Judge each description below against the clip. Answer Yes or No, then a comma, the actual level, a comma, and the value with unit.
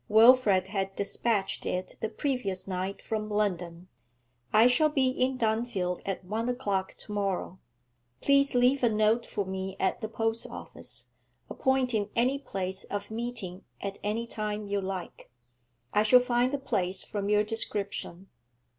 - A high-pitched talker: Yes, high, 210 Hz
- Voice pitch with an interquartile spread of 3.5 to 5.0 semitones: Yes, average, 3.9 semitones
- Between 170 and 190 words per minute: No, average, 150 wpm